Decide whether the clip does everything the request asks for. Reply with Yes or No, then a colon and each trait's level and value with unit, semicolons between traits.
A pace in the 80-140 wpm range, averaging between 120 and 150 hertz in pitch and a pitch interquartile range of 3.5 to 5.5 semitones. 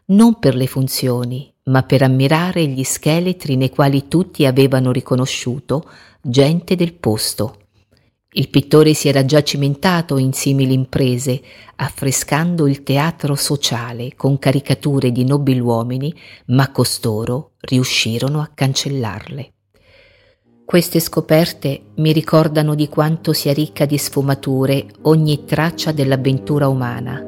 No: average, 120 wpm; medium, 140 Hz; average, 2.9 semitones